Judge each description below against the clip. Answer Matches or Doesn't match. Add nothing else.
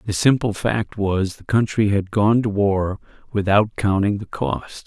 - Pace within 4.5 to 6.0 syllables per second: Doesn't match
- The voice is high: Doesn't match